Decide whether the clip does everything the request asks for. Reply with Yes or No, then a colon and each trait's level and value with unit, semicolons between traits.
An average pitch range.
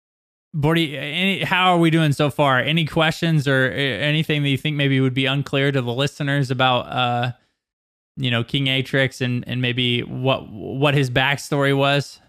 No: narrow, 2.3 semitones